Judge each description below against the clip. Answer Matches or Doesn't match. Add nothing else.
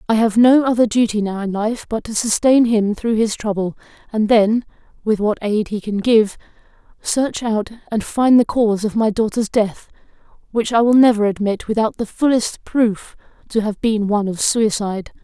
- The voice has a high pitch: Matches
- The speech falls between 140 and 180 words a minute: Doesn't match